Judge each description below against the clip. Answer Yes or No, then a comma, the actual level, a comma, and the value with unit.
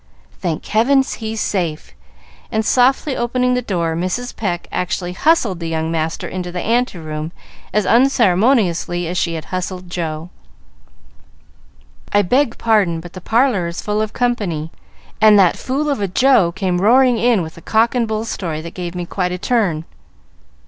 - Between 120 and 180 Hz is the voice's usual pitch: No, high, 190 Hz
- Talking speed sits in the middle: Yes, average, 170 wpm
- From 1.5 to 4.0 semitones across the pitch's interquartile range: No, wide, 5.4 semitones